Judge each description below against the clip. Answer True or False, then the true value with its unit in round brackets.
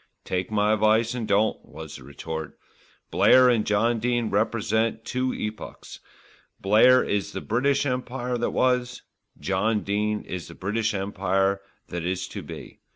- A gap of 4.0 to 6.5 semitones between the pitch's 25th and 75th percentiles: False (3.5 semitones)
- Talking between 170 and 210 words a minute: False (150 wpm)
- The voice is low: True (110 Hz)